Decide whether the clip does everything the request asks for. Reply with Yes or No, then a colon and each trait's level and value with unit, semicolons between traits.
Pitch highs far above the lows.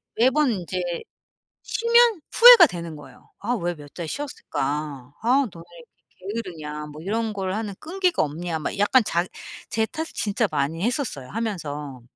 Yes: wide, 7.8 semitones